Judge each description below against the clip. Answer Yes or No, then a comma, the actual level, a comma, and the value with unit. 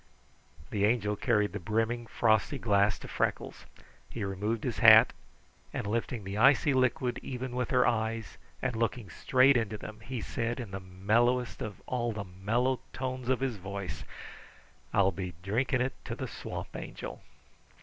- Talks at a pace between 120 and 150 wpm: No, average, 160 wpm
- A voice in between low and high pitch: No, low, 115 Hz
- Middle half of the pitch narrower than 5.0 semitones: Yes, average, 3.6 semitones